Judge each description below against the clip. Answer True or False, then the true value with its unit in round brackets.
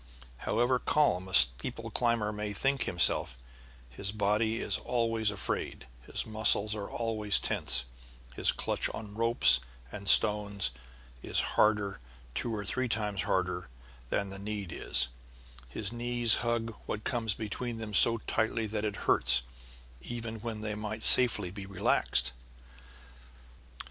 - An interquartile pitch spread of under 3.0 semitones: True (2.4 semitones)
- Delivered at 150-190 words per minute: False (140 wpm)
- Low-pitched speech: True (105 Hz)